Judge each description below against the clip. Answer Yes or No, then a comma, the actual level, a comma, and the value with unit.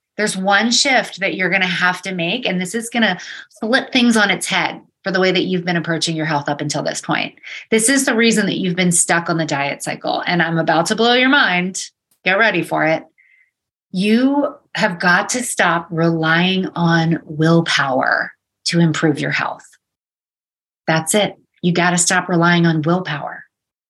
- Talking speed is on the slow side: No, average, 195 wpm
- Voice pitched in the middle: Yes, medium, 180 Hz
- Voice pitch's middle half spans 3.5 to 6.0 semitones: Yes, average, 4.2 semitones